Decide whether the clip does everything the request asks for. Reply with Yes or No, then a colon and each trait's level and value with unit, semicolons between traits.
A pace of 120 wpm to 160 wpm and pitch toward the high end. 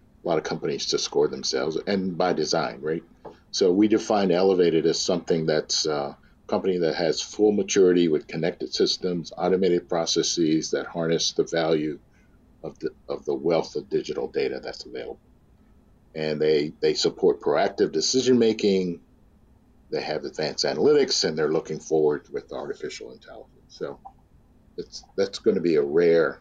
Yes: average, 155 wpm; very high, 395 Hz